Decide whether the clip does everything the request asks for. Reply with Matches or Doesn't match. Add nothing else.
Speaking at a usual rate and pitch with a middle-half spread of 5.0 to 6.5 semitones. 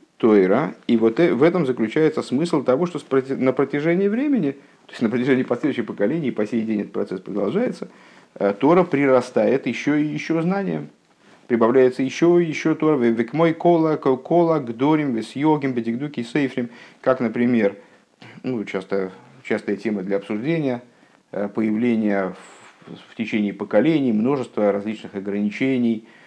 Matches